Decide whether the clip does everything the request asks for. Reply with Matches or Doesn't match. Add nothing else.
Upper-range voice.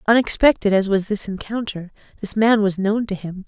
Matches